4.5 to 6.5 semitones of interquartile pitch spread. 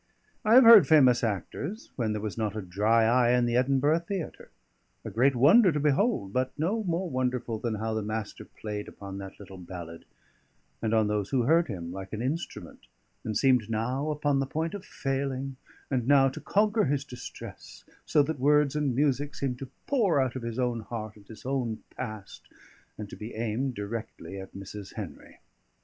Yes: average, 5.0 semitones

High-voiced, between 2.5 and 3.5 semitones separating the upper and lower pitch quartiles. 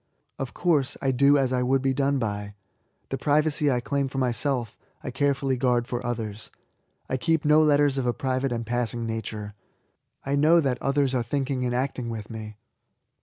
No: low, 130 Hz; average, 2.8 semitones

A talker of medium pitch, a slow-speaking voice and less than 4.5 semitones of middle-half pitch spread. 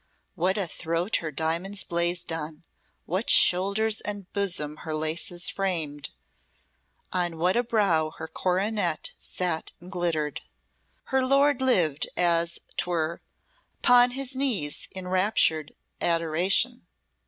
Yes: medium, 180 Hz; slow, 120 wpm; average, 3.9 semitones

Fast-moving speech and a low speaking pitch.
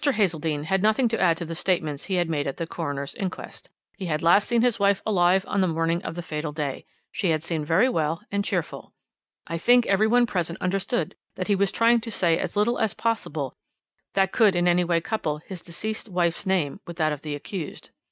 No: fast, 220 wpm; medium, 175 Hz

